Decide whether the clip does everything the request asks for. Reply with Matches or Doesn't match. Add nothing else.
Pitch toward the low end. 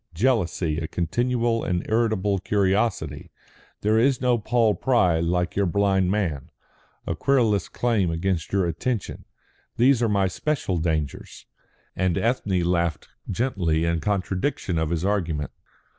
Matches